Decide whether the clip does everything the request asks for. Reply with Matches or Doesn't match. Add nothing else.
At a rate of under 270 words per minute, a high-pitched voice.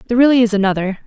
Matches